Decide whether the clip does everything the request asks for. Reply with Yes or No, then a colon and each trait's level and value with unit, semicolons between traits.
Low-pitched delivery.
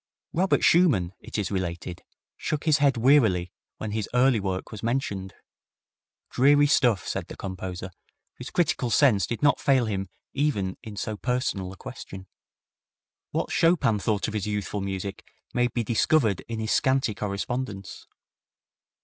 Yes: low, 110 Hz